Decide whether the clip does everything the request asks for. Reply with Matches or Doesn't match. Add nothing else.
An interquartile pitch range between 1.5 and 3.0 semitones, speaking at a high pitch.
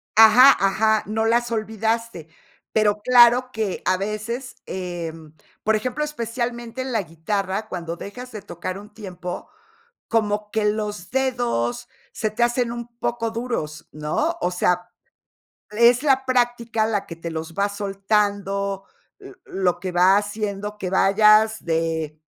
Doesn't match